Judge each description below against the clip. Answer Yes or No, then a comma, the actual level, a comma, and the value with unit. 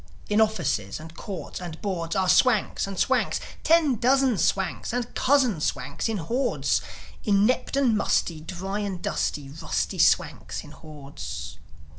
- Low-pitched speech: No, high, 195 Hz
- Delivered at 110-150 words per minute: Yes, average, 140 wpm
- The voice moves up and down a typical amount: No, wide, 6.7 semitones